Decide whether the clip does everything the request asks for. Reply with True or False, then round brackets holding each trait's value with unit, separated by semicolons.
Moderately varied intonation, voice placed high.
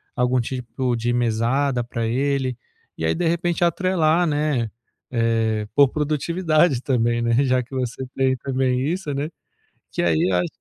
False (4.1 semitones; 130 Hz)